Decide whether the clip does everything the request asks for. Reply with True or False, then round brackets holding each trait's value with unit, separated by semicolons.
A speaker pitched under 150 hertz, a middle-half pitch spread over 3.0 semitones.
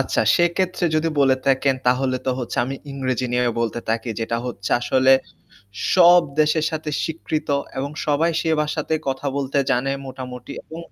True (135 Hz; 3.6 semitones)